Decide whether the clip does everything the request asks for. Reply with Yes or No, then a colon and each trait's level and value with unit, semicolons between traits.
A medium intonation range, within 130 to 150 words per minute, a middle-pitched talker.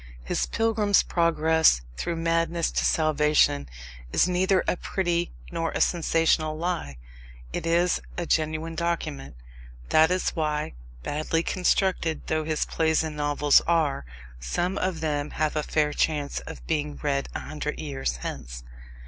No: narrow, 2.3 semitones; average, 140 wpm; medium, 160 Hz